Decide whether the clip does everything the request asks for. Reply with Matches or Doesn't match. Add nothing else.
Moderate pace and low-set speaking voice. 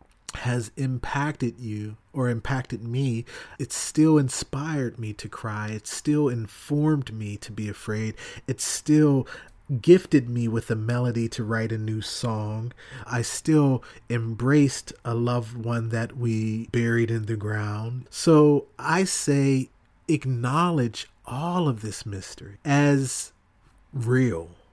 Doesn't match